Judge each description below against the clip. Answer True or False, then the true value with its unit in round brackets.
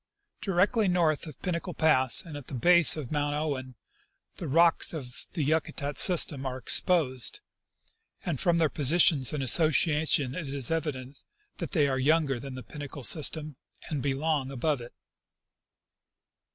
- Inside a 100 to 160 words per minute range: True (150 wpm)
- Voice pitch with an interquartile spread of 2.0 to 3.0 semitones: False (3.4 semitones)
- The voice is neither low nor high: True (150 Hz)